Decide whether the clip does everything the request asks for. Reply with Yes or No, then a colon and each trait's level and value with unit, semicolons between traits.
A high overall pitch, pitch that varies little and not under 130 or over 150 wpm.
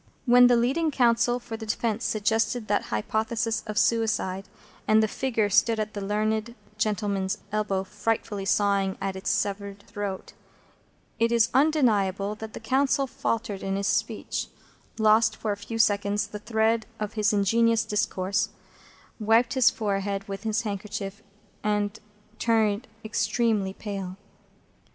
Yes: high, 215 Hz; narrow, 2.1 semitones; average, 140 wpm